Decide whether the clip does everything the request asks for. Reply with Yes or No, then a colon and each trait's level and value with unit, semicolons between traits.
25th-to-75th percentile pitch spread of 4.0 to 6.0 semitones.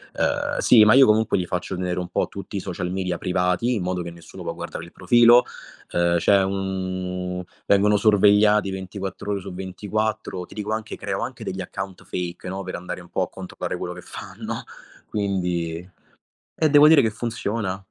No: average, 2.7 semitones